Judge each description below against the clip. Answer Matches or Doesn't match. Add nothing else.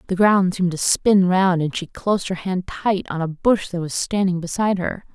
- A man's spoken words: Doesn't match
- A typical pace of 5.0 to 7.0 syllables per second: Matches